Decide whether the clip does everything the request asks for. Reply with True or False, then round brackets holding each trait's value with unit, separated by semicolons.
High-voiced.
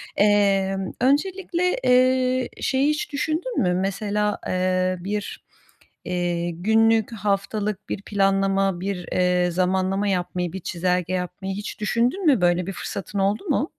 True (195 Hz)